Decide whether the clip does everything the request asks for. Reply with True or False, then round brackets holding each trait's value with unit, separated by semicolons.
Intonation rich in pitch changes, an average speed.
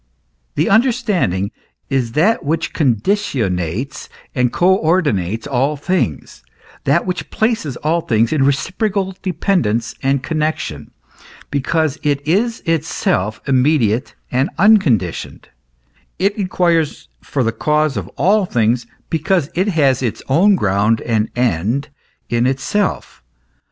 False (7.4 semitones; 115 wpm)